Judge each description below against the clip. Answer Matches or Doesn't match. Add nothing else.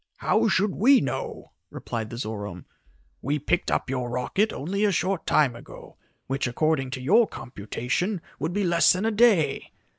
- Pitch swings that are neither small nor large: Doesn't match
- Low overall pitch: Doesn't match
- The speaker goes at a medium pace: Matches